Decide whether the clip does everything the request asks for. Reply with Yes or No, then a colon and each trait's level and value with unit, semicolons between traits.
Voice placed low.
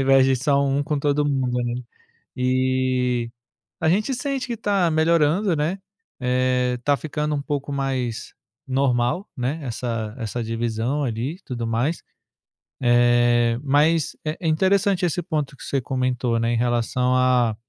Yes: low, 130 Hz